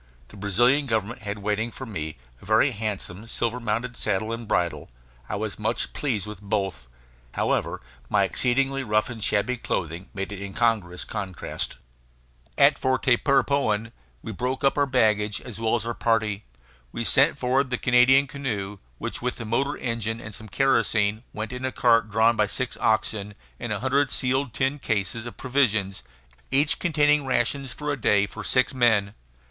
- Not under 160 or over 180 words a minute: Yes, average, 170 wpm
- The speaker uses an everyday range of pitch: Yes, average, 3.9 semitones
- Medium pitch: No, low, 115 Hz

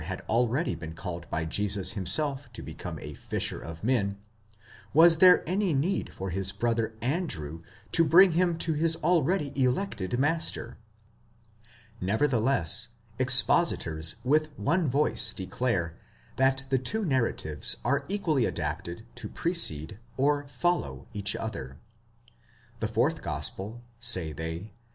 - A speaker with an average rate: No, slow, 130 wpm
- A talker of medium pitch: No, low, 120 Hz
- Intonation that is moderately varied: No, wide, 8.6 semitones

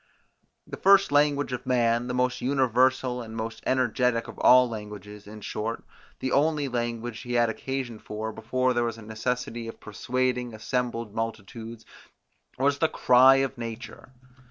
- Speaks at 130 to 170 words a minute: Yes, average, 155 wpm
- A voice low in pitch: Yes, low, 120 Hz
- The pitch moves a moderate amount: No, narrow, 2.3 semitones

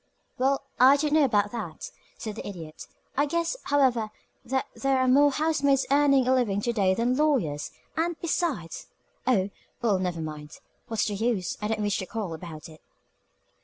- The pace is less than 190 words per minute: Yes, average, 175 wpm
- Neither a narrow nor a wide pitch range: No, wide, 6.3 semitones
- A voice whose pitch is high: Yes, high, 235 Hz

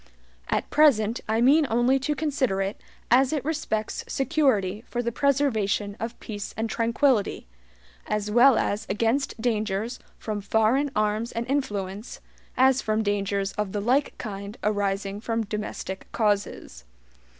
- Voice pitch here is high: Yes, high, 220 Hz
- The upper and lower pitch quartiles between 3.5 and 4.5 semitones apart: Yes, average, 4.1 semitones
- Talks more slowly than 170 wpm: Yes, average, 140 wpm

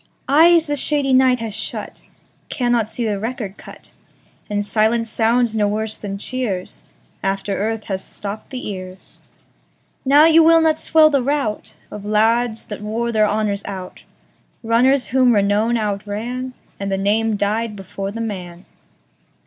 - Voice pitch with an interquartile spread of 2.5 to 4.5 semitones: Yes, average, 3.6 semitones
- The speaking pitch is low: No, high, 220 Hz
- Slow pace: Yes, slow, 130 wpm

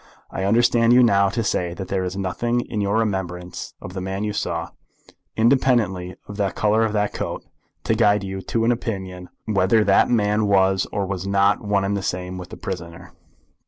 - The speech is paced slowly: No, average, 200 wpm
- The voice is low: Yes, low, 100 Hz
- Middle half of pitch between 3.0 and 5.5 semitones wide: No, narrow, 2.5 semitones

